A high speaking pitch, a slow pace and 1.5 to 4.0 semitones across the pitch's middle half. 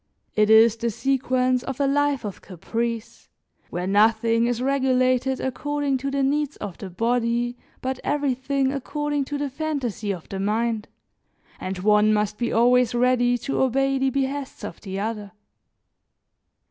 No: high, 245 Hz; average, 150 wpm; average, 3.6 semitones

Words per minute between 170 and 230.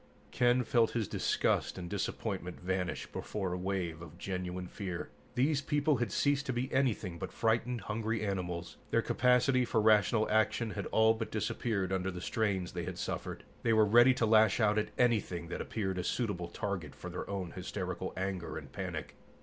Yes: average, 180 wpm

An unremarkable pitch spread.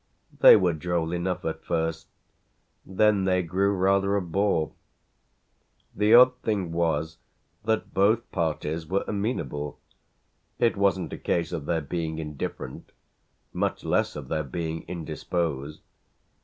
Yes: average, 3.5 semitones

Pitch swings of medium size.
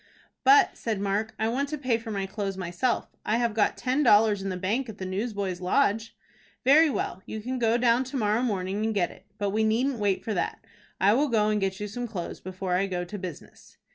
Yes: average, 3.6 semitones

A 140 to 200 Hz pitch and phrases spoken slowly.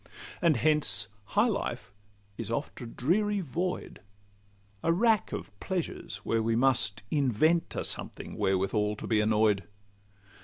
No: low, 130 Hz; slow, 130 wpm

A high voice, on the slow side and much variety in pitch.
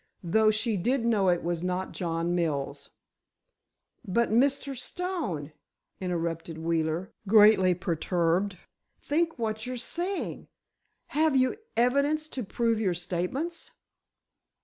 Yes: high, 205 Hz; slow, 105 wpm; wide, 6.8 semitones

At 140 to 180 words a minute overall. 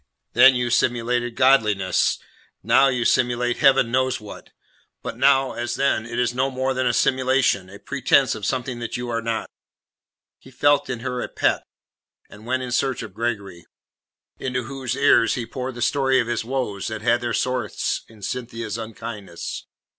Yes: average, 175 wpm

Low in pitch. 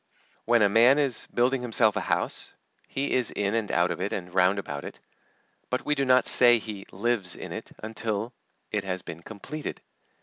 Yes: low, 110 Hz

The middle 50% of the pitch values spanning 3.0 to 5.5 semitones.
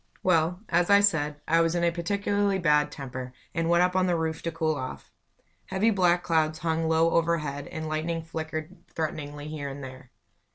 No: narrow, 2.4 semitones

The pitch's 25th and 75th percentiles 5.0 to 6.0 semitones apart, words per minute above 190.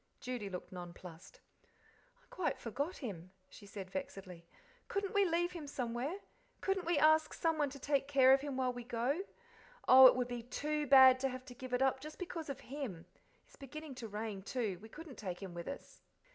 Yes: average, 5.3 semitones; average, 200 wpm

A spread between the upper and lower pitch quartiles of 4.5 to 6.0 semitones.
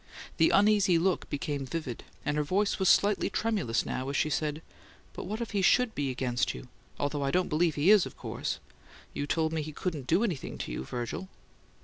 Yes: average, 5.1 semitones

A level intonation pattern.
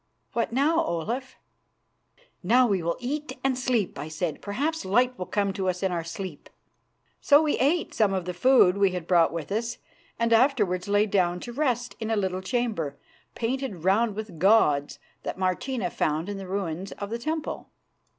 No: wide, 5.4 semitones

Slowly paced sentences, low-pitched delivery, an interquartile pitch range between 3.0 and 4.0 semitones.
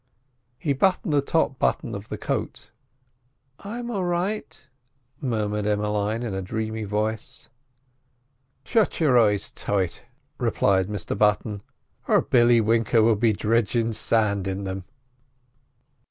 Yes: slow, 120 wpm; low, 110 Hz; average, 3.7 semitones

